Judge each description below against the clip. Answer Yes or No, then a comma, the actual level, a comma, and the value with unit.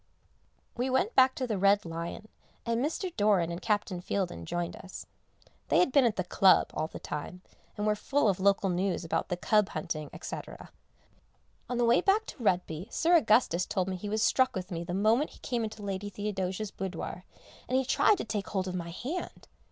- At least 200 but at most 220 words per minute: Yes, fast, 205 wpm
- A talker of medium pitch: No, high, 200 Hz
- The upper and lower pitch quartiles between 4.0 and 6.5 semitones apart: Yes, average, 4.7 semitones